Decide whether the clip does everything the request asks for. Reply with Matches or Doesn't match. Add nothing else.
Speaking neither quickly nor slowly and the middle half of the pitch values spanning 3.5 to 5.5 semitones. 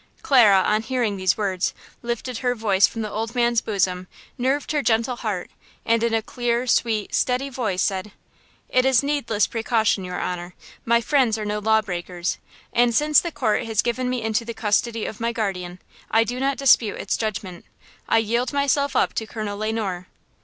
Doesn't match